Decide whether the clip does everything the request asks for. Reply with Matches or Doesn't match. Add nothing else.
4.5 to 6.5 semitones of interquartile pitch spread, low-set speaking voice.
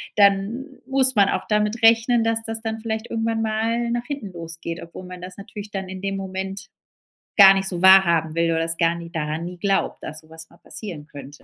Doesn't match